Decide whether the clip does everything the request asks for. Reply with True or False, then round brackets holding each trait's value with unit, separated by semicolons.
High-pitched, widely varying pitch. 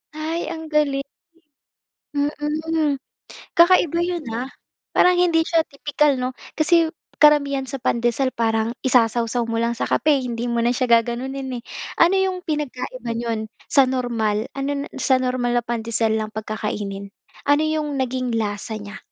False (255 Hz; 4.5 semitones)